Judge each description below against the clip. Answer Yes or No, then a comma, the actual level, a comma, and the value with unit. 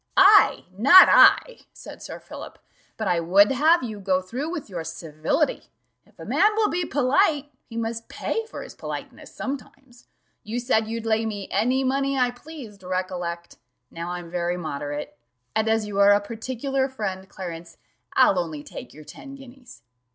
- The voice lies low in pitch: No, high, 225 Hz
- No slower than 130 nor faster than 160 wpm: No, average, 170 wpm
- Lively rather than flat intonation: Yes, wide, 6.8 semitones